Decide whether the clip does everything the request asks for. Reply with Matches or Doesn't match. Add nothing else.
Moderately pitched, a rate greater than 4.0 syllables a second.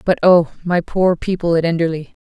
Matches